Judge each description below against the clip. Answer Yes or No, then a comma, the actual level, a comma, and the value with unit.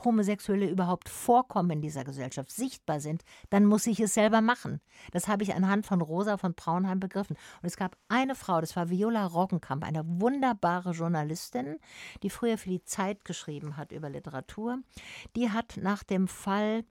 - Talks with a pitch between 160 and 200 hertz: Yes, high, 190 Hz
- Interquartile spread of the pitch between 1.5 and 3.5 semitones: No, average, 4.4 semitones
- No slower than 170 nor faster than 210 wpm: Yes, average, 175 wpm